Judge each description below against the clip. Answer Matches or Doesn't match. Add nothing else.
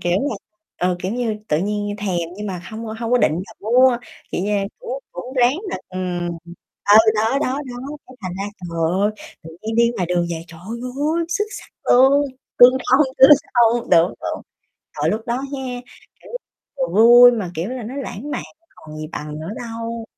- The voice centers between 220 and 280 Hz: Matches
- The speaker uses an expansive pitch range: Matches